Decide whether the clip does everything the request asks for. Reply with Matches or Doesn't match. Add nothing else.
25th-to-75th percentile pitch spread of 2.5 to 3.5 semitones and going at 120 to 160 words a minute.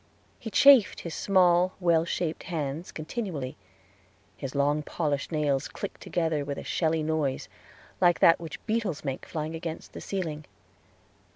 Matches